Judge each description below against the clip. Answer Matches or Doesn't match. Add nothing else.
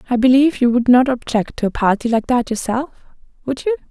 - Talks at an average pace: Doesn't match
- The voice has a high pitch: Matches